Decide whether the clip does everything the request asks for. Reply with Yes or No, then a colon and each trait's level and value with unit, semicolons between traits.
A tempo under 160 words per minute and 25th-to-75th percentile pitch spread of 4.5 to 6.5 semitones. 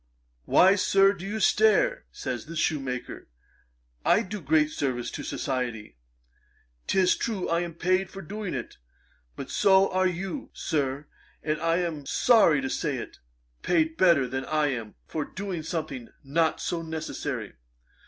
Yes: average, 150 wpm; average, 5.2 semitones